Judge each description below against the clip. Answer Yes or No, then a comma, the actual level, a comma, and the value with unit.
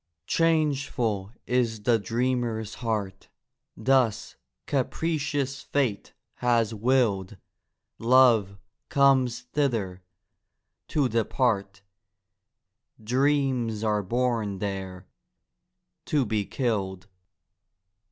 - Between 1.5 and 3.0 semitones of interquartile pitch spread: No, average, 4.4 semitones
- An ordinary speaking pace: No, slow, 65 wpm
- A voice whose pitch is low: Yes, low, 115 Hz